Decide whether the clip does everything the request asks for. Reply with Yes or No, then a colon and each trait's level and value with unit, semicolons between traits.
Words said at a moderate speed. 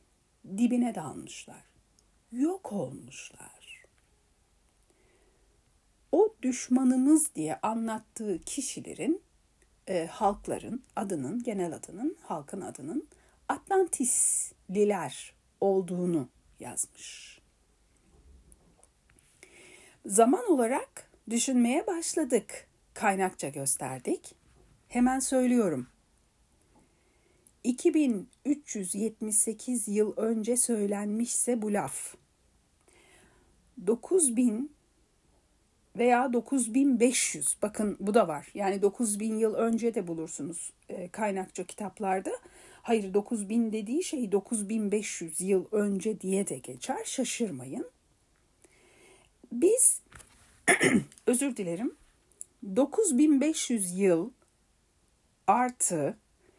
No: slow, 70 wpm